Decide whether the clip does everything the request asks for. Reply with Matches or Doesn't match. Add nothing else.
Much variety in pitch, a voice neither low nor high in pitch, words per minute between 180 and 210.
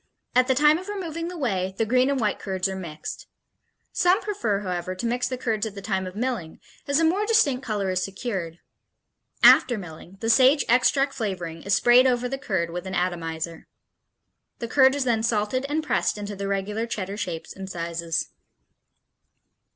Doesn't match